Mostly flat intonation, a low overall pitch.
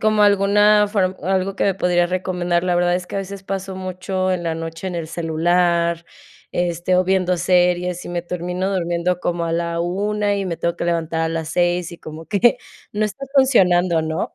No: narrow, 2.0 semitones; medium, 180 Hz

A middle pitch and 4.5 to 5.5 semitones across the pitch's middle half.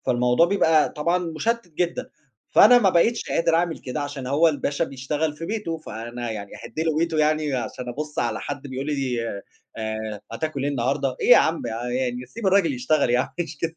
Yes: medium, 145 Hz; average, 4.8 semitones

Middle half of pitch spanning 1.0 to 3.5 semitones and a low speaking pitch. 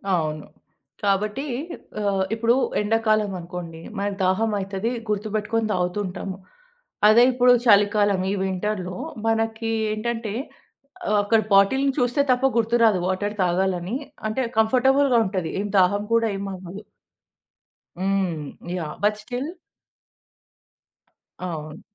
No: average, 3.2 semitones; high, 205 Hz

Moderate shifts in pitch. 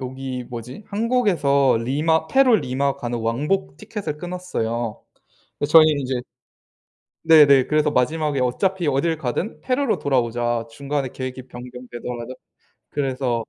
Yes: average, 4.5 semitones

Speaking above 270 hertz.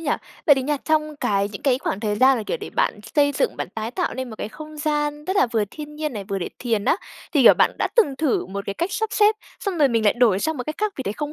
Yes: very high, 285 Hz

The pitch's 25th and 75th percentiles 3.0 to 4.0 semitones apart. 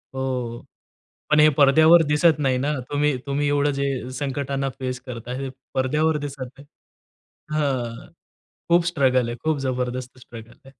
No: narrow, 2.6 semitones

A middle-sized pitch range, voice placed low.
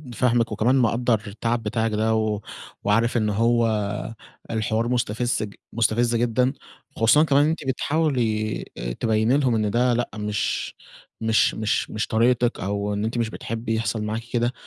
No: narrow, 2.0 semitones; low, 115 Hz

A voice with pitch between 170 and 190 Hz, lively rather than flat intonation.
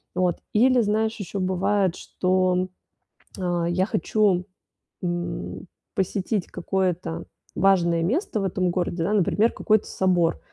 No: medium, 185 Hz; narrow, 2.6 semitones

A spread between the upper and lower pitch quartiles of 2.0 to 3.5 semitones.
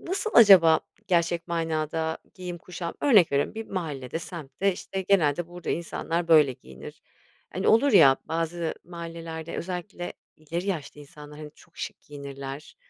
Yes: average, 2.8 semitones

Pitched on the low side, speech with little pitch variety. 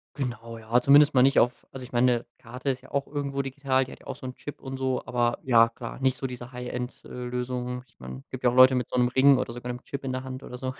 Yes: low, 125 Hz; narrow, 1.4 semitones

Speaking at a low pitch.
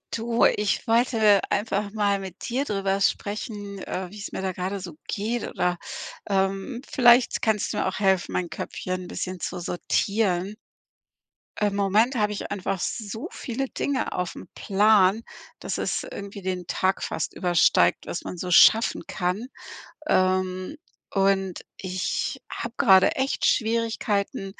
No: high, 200 Hz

